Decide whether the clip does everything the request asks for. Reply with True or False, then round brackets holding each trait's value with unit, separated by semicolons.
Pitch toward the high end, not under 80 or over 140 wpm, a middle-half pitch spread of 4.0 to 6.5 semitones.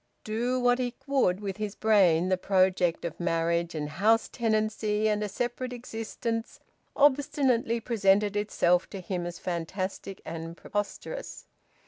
True (210 Hz; 135 wpm; 4.4 semitones)